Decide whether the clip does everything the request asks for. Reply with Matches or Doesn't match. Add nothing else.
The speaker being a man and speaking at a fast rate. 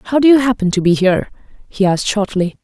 Doesn't match